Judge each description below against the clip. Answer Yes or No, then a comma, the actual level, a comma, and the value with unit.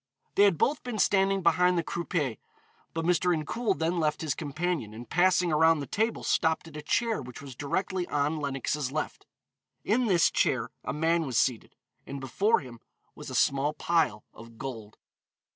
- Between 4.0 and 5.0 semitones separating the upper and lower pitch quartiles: Yes, average, 4.5 semitones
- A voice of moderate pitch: Yes, medium, 160 Hz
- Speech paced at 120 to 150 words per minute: No, average, 175 wpm